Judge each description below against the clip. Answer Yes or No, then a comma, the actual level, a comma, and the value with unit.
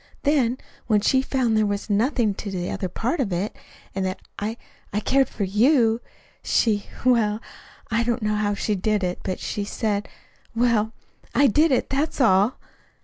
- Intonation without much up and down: No, average, 3.4 semitones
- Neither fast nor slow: Yes, average, 175 wpm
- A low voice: No, high, 215 Hz